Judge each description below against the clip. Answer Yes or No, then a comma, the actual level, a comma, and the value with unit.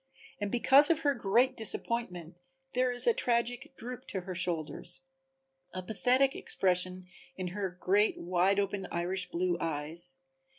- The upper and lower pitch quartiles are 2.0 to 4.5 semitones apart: No, wide, 5.5 semitones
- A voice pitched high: Yes, high, 195 Hz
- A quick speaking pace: No, average, 140 wpm